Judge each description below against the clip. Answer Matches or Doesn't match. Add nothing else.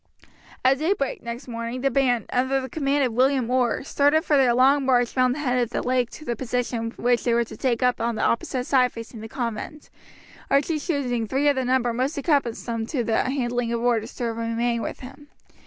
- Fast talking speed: Matches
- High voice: Matches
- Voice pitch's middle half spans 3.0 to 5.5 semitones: Doesn't match